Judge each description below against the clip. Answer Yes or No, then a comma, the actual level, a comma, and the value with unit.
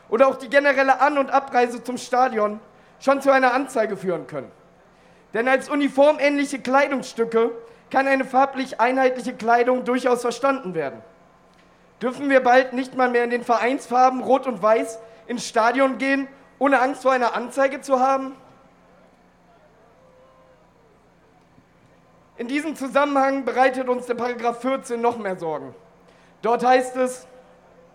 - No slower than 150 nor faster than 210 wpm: No, average, 135 wpm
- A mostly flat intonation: Yes, narrow, 2.2 semitones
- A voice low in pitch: No, very high, 255 Hz